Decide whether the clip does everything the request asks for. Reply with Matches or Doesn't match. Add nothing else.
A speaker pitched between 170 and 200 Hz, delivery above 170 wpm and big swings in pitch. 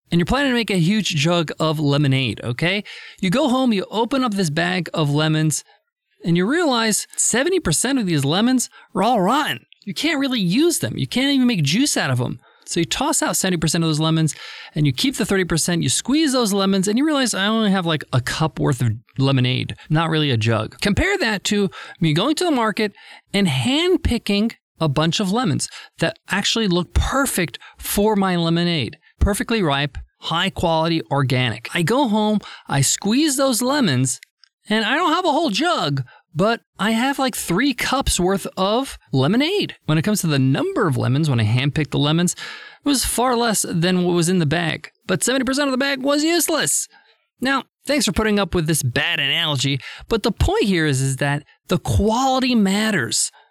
Matches